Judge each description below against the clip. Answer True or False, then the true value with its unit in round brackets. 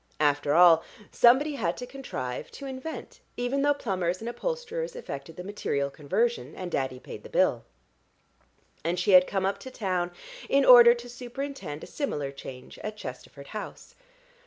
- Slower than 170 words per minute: True (160 wpm)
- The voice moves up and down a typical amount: False (8.4 semitones)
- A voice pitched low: False (205 Hz)